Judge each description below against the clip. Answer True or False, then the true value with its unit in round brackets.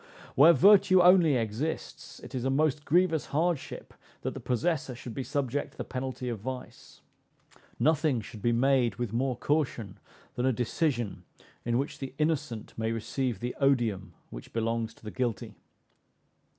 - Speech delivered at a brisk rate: False (160 wpm)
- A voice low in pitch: True (130 Hz)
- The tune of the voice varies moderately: True (4.4 semitones)